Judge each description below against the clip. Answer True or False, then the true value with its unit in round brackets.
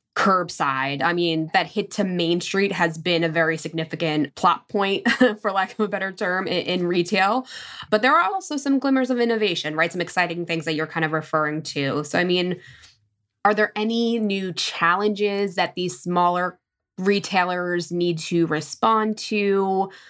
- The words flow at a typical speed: True (170 wpm)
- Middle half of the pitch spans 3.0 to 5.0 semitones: True (3.6 semitones)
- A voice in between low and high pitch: True (180 Hz)